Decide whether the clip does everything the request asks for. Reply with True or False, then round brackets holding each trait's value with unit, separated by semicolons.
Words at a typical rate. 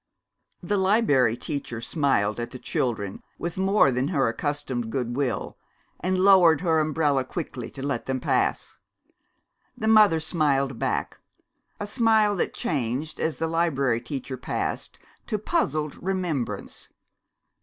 False (130 wpm)